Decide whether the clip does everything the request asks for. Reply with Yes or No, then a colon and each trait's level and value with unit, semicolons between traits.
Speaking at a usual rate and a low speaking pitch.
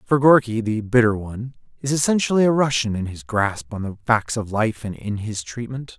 No: fast, 210 wpm; low, 115 Hz